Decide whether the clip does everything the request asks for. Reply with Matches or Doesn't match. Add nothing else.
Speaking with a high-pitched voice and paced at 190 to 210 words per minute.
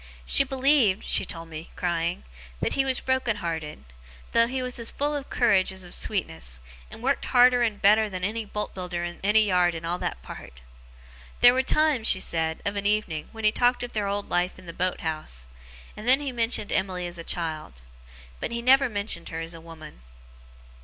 Matches